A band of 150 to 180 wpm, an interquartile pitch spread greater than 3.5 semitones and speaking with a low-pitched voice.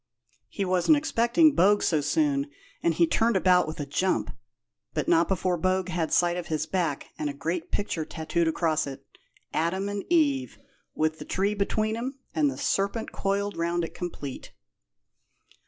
No: average, 170 wpm; average, 4.0 semitones; medium, 180 Hz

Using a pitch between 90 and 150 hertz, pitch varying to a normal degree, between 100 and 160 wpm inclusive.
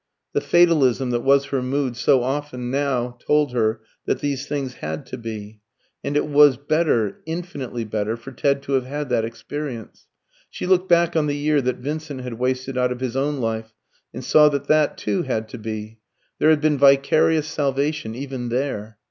No: low, 135 Hz; average, 3.5 semitones; average, 190 wpm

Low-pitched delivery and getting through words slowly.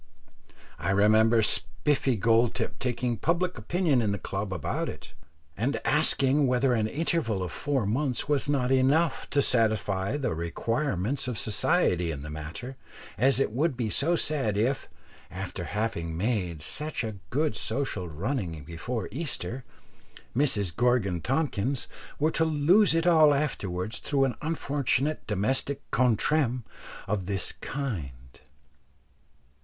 Yes: low, 120 Hz; slow, 130 wpm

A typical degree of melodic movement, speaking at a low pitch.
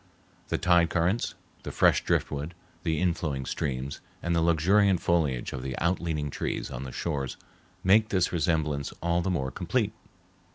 Yes: average, 3.7 semitones; very low, 80 Hz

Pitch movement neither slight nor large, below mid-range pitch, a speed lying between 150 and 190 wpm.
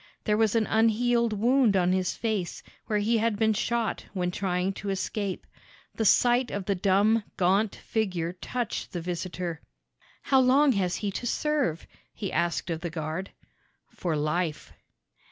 No: average, 4.1 semitones; high, 200 Hz; average, 155 wpm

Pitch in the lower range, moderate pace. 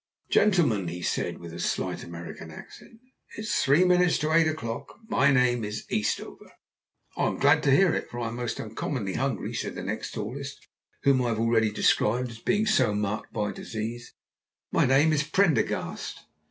Yes: low, 125 Hz; average, 175 wpm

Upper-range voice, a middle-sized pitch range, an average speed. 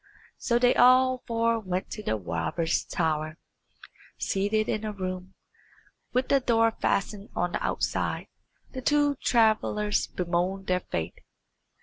No: high, 210 Hz; average, 4.6 semitones; slow, 130 wpm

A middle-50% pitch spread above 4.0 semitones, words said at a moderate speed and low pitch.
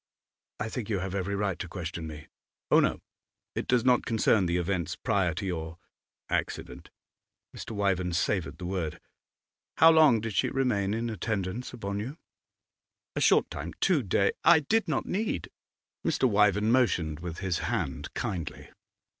Yes: average, 4.8 semitones; average, 165 wpm; low, 100 Hz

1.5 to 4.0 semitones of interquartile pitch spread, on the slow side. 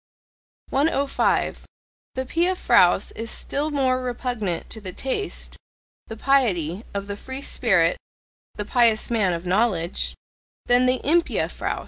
No: average, 5.3 semitones; slow, 130 wpm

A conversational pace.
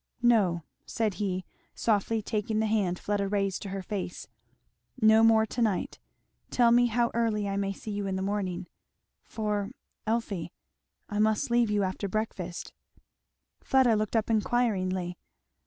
Yes: average, 150 wpm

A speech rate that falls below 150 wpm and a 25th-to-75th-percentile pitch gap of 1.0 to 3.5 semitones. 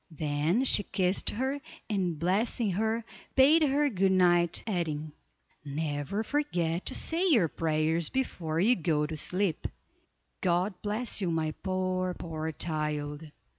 No: slow, 135 wpm; wide, 5.4 semitones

